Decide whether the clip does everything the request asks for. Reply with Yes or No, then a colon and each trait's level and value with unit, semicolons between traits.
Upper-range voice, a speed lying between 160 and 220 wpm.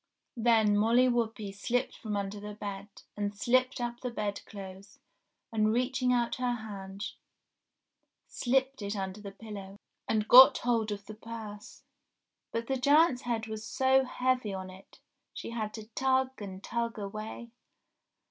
No: high, 220 Hz; average, 150 wpm